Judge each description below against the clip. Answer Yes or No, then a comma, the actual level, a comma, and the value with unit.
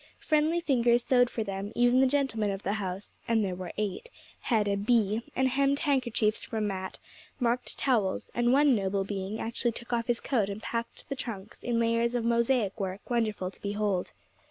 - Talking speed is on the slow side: No, average, 190 wpm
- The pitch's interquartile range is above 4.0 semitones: No, average, 3.4 semitones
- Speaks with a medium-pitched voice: No, high, 230 Hz